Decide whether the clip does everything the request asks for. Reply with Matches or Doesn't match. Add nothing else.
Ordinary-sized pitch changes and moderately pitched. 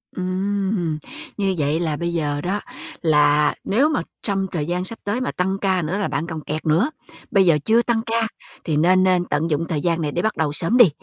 Matches